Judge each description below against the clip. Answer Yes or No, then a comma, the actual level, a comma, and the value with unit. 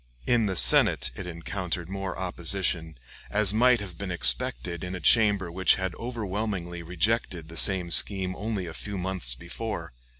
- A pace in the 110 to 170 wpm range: Yes, average, 160 wpm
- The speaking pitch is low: Yes, very low, 95 Hz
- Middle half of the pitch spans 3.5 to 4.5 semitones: No, average, 3.1 semitones